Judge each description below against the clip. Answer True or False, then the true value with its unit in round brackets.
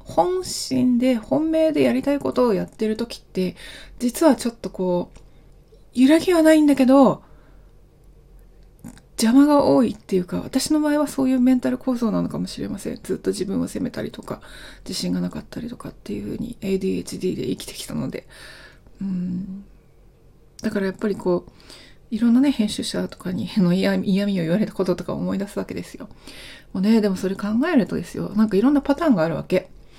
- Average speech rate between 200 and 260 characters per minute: False (370 characters per minute)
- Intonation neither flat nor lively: False (5.7 semitones)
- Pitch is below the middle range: False (220 Hz)